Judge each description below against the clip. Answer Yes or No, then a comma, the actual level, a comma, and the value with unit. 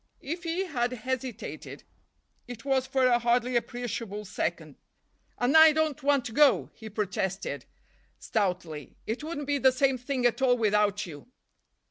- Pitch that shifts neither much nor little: Yes, average, 4.1 semitones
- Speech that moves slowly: No, average, 150 wpm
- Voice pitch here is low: No, high, 245 Hz